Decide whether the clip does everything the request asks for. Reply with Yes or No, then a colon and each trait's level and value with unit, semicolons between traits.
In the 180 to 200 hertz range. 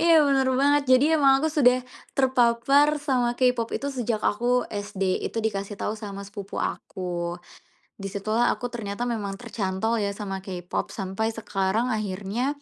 No: high, 225 Hz